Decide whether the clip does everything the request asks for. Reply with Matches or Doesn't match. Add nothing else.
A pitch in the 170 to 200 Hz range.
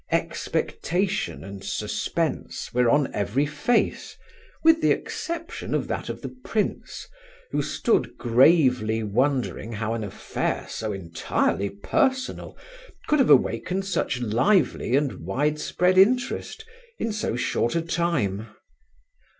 Doesn't match